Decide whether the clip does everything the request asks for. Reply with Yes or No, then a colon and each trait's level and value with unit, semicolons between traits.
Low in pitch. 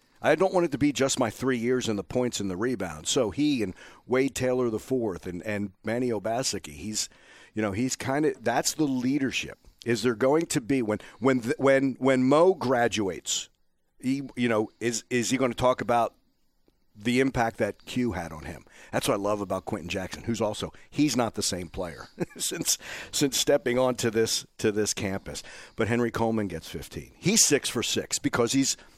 Yes: low, 120 Hz